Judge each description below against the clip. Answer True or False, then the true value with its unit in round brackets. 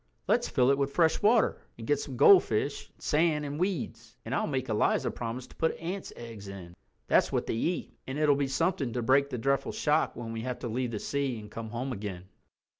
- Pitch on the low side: True (130 Hz)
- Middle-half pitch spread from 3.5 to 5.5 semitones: True (4.5 semitones)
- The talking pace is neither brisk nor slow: False (215 wpm)